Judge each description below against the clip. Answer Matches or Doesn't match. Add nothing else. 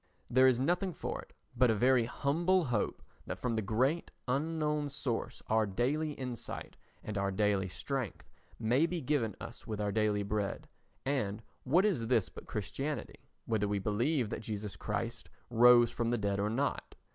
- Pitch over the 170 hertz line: Doesn't match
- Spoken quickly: Doesn't match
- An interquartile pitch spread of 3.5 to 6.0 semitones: Matches